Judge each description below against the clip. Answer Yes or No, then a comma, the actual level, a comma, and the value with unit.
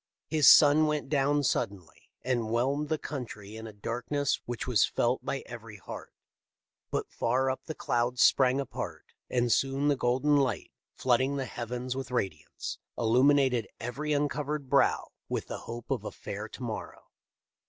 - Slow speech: No, average, 160 wpm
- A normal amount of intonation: Yes, average, 3.1 semitones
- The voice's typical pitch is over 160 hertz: No, low, 130 Hz